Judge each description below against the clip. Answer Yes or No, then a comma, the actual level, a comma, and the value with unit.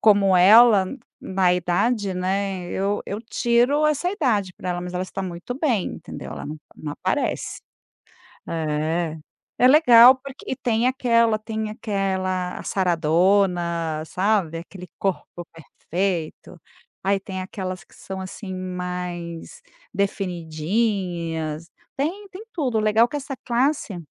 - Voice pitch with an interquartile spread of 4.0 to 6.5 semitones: Yes, average, 4.7 semitones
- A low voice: No, high, 195 Hz